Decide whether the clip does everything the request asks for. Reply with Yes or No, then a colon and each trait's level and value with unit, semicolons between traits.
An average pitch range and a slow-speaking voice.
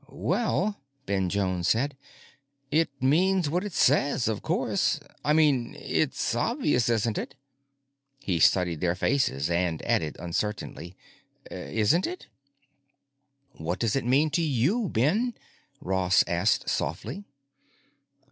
No: wide, 9.0 semitones; slow, 120 wpm